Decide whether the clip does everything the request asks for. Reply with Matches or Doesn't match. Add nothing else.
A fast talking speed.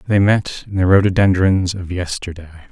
Doesn't match